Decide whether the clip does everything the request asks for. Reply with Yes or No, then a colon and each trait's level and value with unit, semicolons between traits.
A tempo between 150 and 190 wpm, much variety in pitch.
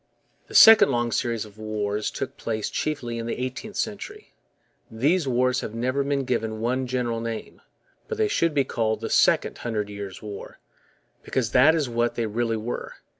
No: average, 175 wpm; average, 3.5 semitones